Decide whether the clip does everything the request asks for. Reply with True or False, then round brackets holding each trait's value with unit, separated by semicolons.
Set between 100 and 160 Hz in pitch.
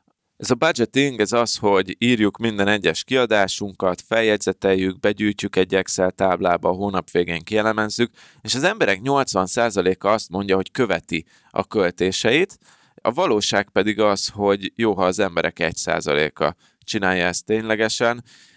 True (105 Hz)